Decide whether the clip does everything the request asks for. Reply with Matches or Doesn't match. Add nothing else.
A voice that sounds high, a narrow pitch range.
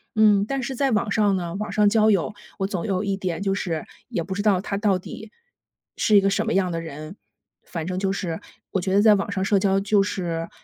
Matches